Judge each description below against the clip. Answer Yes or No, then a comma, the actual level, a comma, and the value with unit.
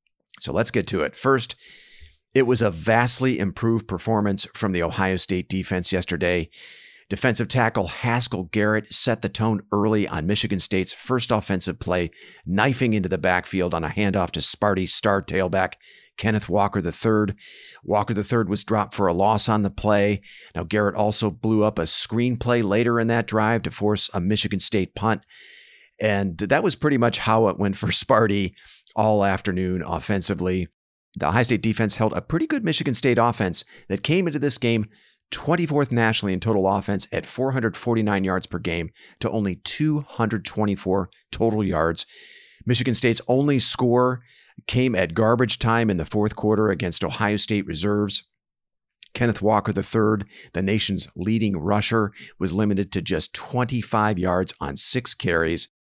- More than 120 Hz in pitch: No, low, 105 Hz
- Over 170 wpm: No, average, 160 wpm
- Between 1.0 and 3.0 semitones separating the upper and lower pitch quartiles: No, average, 3.4 semitones